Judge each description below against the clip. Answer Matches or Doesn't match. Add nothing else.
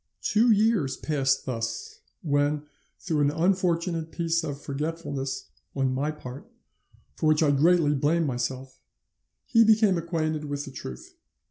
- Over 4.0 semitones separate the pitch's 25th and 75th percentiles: Doesn't match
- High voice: Doesn't match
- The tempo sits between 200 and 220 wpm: Doesn't match